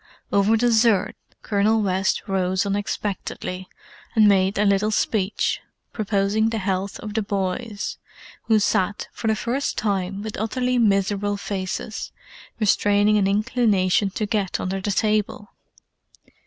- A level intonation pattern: Yes, narrow, 1.9 semitones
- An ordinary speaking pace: No, slow, 130 wpm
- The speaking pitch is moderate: No, high, 205 Hz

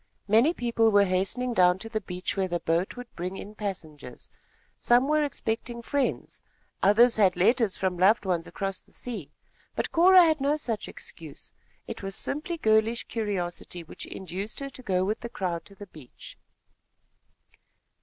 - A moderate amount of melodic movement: Yes, average, 4.7 semitones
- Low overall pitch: No, high, 210 Hz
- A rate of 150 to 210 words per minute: Yes, average, 165 wpm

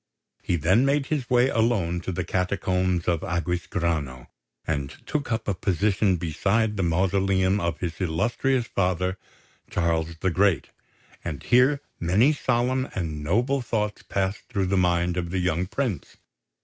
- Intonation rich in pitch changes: No, average, 4.6 semitones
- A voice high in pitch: No, very low, 95 Hz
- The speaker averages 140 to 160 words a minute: Yes, average, 150 wpm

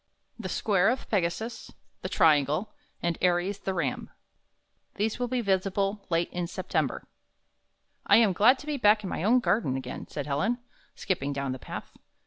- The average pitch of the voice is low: No, high, 190 Hz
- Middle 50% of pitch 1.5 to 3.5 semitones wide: No, average, 4.8 semitones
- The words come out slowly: No, average, 165 wpm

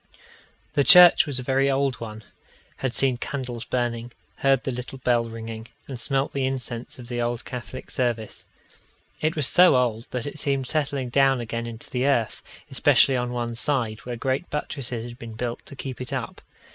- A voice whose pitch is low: Yes, low, 125 Hz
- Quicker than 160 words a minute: Yes, average, 185 wpm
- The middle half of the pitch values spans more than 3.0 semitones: No, narrow, 2.5 semitones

